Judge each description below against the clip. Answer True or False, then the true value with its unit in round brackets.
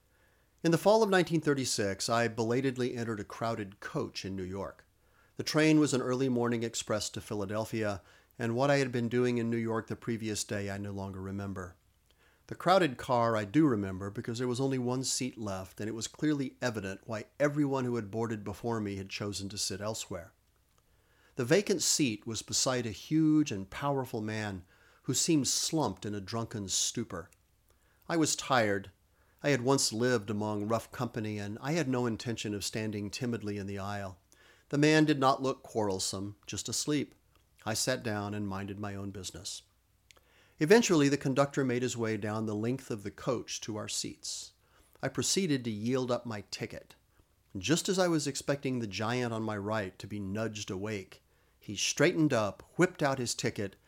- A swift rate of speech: False (185 wpm)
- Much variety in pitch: False (4.4 semitones)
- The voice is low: True (110 Hz)